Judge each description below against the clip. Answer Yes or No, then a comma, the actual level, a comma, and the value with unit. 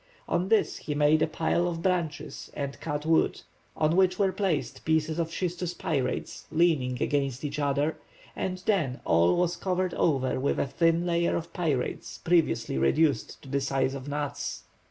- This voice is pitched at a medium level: Yes, medium, 155 Hz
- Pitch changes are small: No, average, 3.7 semitones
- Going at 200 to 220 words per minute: No, average, 170 wpm